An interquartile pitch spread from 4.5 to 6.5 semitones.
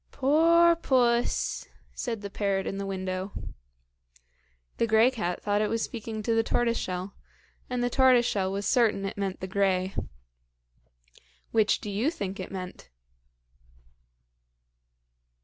No: average, 3.7 semitones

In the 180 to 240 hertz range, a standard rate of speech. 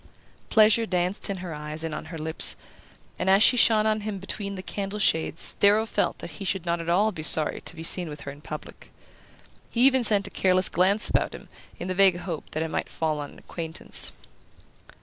No: medium, 185 Hz; fast, 220 wpm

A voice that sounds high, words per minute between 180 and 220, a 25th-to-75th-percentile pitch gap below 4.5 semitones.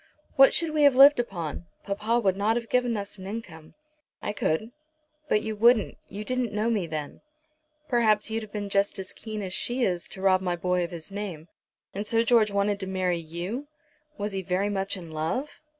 Yes: high, 205 Hz; fast, 205 wpm; average, 3.7 semitones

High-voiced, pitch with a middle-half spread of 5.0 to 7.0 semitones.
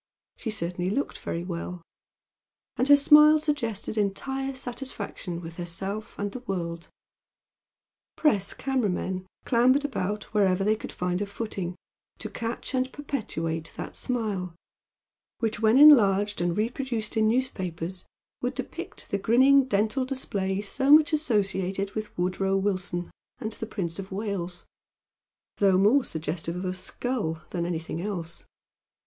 Yes: high, 205 Hz; wide, 5.6 semitones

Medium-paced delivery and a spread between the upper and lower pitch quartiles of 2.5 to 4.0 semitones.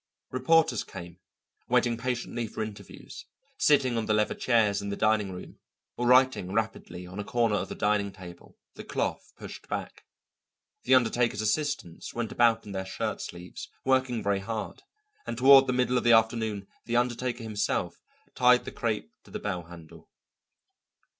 Yes: average, 165 wpm; average, 3.4 semitones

